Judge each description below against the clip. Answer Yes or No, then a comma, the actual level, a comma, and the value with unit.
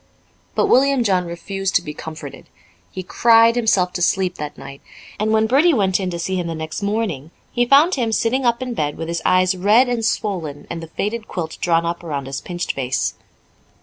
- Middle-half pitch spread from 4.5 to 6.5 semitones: Yes, wide, 5.4 semitones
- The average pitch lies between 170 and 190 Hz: Yes, medium, 185 Hz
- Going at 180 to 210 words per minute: Yes, fast, 205 wpm